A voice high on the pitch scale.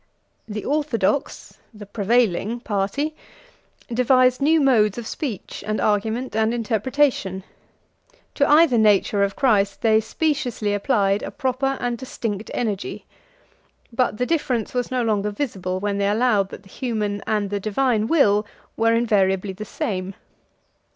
Yes: high, 220 Hz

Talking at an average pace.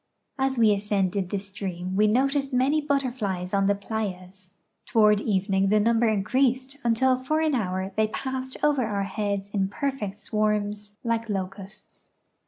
Yes: average, 150 wpm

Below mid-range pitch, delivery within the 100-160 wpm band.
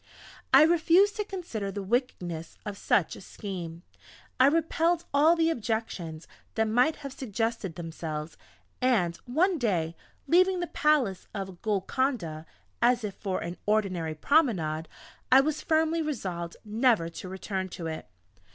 No: high, 220 Hz; average, 140 wpm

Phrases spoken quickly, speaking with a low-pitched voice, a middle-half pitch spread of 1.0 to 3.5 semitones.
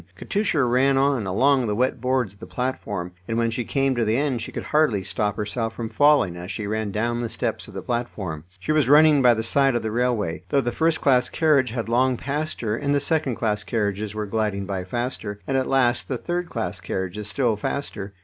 No: fast, 225 wpm; low, 120 Hz; average, 4.3 semitones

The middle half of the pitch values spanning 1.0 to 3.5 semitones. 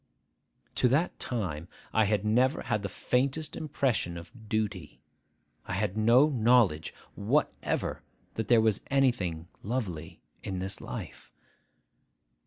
No: average, 5.0 semitones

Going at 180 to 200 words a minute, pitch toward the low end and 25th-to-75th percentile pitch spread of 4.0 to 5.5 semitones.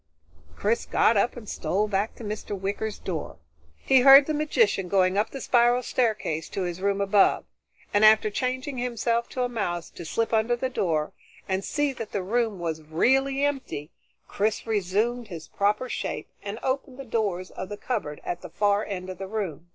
No: average, 190 wpm; high, 215 Hz; average, 4.4 semitones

